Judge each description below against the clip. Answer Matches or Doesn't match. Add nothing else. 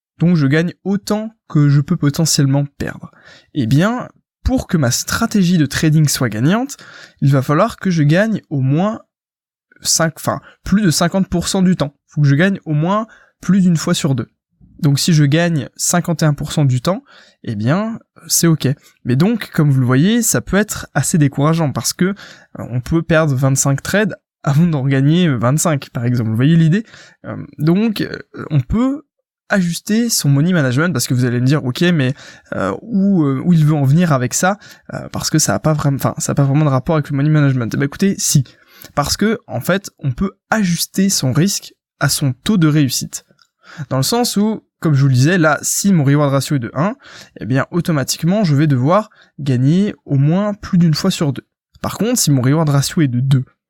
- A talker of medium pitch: Matches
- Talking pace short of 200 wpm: Doesn't match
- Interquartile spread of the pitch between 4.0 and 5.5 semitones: Matches